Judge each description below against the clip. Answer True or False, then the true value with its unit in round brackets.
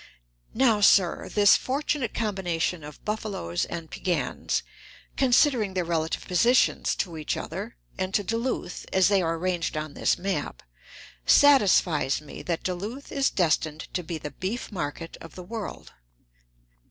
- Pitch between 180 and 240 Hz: True (185 Hz)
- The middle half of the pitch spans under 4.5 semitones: False (4.9 semitones)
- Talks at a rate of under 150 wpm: True (140 wpm)